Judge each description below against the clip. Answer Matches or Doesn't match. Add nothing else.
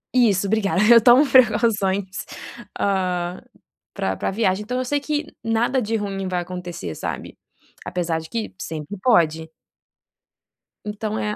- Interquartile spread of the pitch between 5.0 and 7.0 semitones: Doesn't match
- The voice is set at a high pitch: Matches